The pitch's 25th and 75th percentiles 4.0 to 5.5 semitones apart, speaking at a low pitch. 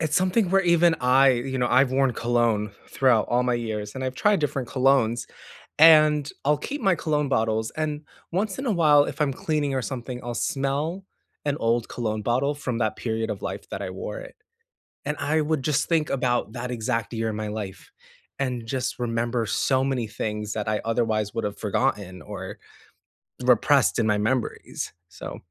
Yes: average, 4.6 semitones; low, 125 Hz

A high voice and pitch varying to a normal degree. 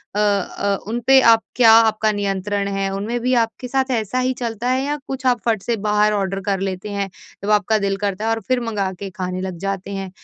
Yes: high, 210 Hz; average, 3.2 semitones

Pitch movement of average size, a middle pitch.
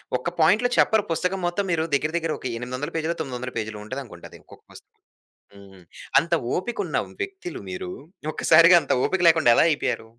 No: wide, 6.3 semitones; medium, 160 Hz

